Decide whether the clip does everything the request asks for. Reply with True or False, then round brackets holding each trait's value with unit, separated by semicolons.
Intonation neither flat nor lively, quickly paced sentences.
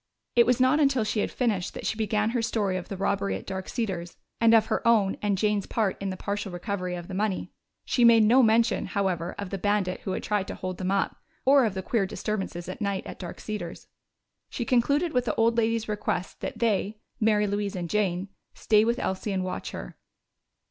True (3.3 semitones; 220 wpm)